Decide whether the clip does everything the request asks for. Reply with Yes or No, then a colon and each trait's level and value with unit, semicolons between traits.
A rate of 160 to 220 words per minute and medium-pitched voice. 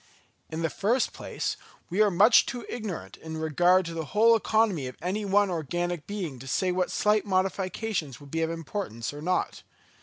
Yes: average, 185 wpm; medium, 180 Hz